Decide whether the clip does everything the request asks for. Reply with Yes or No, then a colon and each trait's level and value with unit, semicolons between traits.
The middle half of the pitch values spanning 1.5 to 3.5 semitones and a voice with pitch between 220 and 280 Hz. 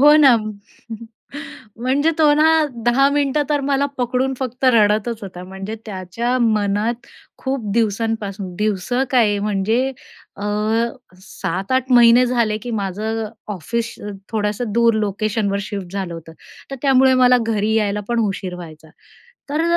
No: average, 3.9 semitones; high, 225 Hz